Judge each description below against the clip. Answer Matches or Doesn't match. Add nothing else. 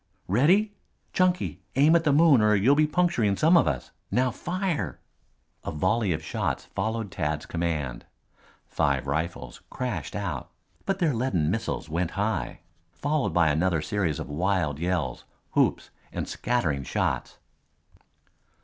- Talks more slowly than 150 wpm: Matches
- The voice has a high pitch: Doesn't match